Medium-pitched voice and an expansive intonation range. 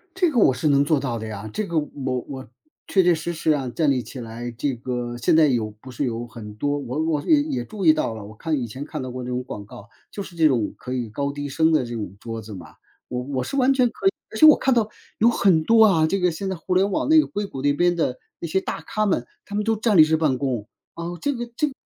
Yes: medium, 145 Hz; wide, 7.6 semitones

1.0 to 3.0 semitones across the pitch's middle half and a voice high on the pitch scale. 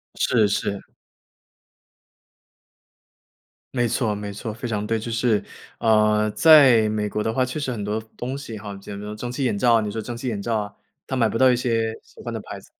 No: narrow, 2.5 semitones; low, 110 Hz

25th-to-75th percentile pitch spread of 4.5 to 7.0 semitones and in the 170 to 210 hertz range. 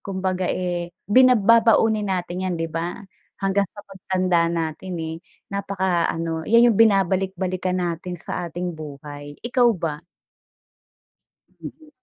No: average, 2.8 semitones; medium, 185 Hz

